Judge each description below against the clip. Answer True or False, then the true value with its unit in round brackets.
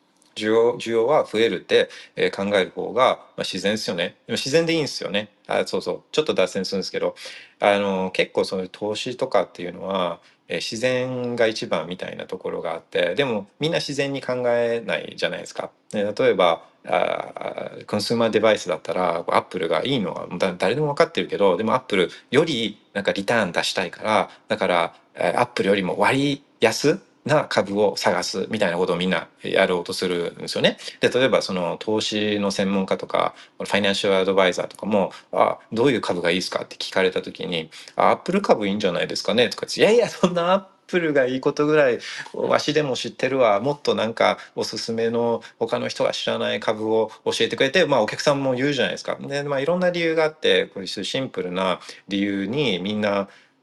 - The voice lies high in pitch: False (130 Hz)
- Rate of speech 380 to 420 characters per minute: True (415 characters per minute)